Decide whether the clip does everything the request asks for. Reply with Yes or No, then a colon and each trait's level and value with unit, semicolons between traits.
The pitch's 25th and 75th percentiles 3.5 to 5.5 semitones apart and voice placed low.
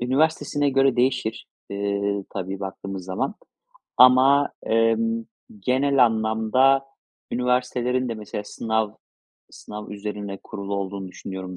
Yes: average, 4.4 semitones; low, 110 Hz